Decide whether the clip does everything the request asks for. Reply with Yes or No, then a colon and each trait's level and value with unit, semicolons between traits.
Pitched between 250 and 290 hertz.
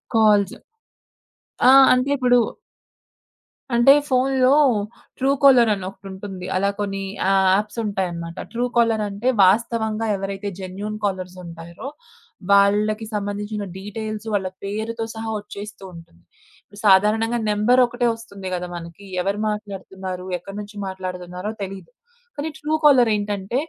No: high, 205 Hz